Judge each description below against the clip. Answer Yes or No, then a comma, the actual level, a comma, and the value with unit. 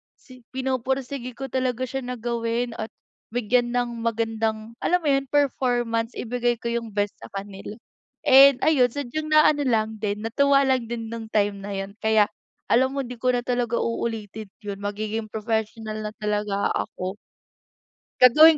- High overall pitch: Yes, high, 235 Hz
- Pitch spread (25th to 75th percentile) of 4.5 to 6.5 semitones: No, average, 2.8 semitones